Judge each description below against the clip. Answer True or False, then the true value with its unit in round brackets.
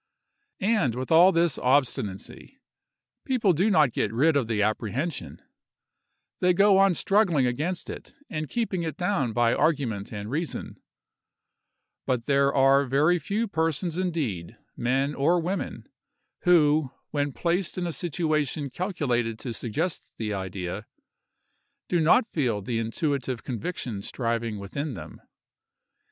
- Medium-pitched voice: True (145 Hz)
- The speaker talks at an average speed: False (130 wpm)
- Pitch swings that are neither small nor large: False (6.7 semitones)